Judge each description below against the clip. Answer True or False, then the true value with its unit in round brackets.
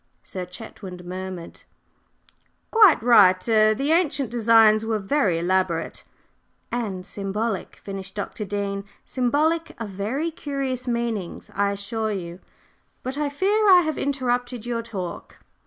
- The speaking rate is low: True (130 wpm)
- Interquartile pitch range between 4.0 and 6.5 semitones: True (5.3 semitones)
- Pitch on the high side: True (225 Hz)